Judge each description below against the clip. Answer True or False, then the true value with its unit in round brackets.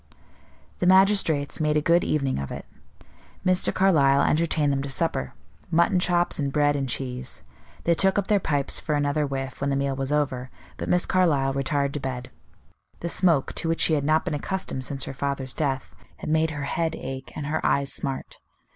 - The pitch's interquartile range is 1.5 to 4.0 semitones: True (3.4 semitones)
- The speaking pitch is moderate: True (145 Hz)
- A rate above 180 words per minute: True (195 wpm)